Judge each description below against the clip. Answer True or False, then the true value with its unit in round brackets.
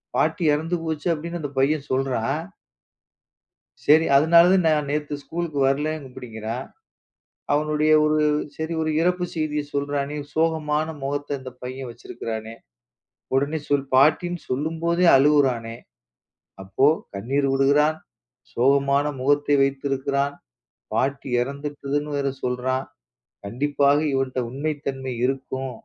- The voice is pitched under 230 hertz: True (140 Hz)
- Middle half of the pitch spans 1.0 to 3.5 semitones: True (2.4 semitones)